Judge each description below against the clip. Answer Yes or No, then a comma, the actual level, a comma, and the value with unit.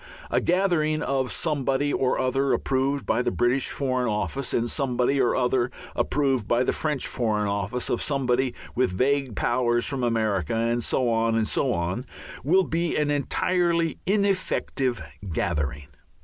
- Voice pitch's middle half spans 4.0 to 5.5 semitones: No, average, 3.2 semitones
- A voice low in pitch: Yes, low, 130 Hz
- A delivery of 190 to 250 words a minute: No, average, 155 wpm